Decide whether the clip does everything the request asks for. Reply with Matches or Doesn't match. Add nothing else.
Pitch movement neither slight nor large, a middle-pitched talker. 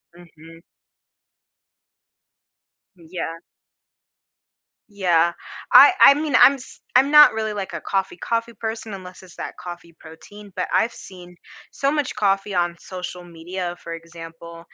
Matches